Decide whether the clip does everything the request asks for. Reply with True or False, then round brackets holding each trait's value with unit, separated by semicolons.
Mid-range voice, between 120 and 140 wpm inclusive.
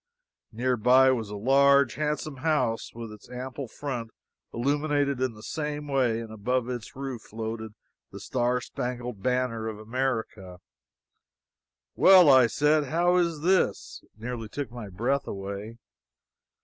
False (125 Hz; 135 wpm)